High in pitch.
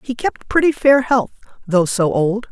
Yes: high, 230 Hz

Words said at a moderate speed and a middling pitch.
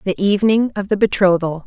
No: average, 180 wpm; high, 195 Hz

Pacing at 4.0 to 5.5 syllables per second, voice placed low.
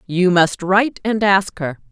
No: 4.2 syllables/s; high, 190 Hz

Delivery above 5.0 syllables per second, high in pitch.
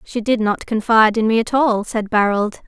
Yes: 5.2 syllables/s; high, 220 Hz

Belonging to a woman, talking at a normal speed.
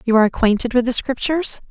No: female; fast, 210 wpm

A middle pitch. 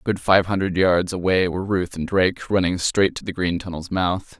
No: very low, 90 Hz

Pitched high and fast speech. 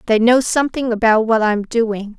No: high, 225 Hz; average, 190 wpm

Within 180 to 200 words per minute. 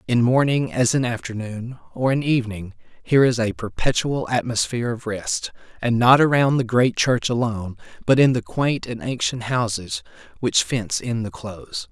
No: average, 170 wpm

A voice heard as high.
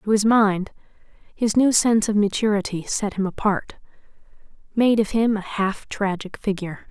Yes: high, 205 Hz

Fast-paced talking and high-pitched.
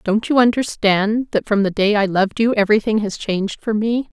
Yes: fast, 215 wpm; high, 210 Hz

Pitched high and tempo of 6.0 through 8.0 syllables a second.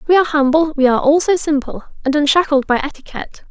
Yes: very high, 295 Hz; 6.9 syllables/s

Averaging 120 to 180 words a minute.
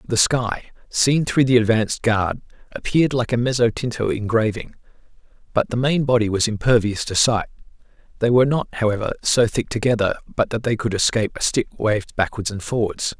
Yes: average, 175 wpm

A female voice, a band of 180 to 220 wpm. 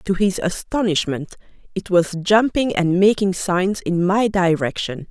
No: female; average, 140 wpm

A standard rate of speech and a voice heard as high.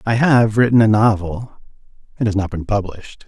No: average, 185 wpm; low, 110 Hz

